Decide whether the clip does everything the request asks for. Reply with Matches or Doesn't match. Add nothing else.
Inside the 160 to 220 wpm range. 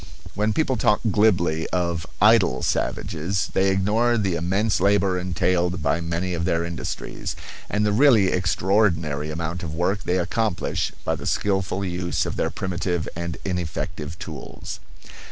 Doesn't match